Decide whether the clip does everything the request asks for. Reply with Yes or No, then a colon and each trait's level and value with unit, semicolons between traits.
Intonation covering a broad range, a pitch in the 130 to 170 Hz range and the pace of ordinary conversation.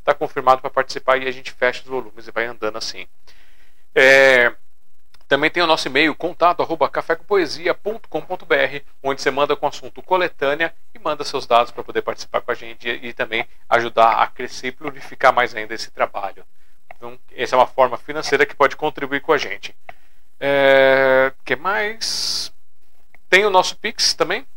No: average, 4.3 semitones; low, 135 Hz; average, 170 wpm